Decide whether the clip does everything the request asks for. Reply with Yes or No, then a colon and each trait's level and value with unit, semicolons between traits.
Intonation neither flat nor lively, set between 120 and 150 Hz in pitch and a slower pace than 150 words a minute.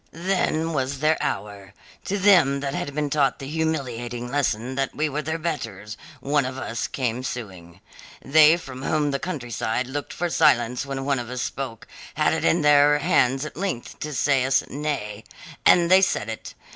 No: average, 3.9 semitones; low, 135 Hz; average, 185 wpm